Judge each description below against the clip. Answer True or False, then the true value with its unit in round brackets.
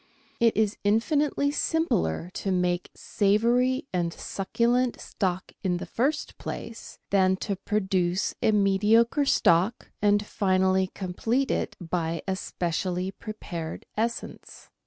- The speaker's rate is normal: False (115 wpm)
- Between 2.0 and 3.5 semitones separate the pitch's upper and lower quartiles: False (4.2 semitones)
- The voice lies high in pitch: True (200 Hz)